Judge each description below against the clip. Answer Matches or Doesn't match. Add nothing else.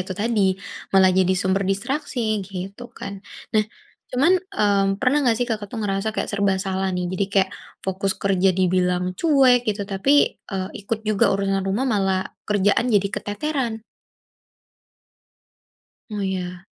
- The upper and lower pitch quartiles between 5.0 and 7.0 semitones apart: Doesn't match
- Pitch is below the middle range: Doesn't match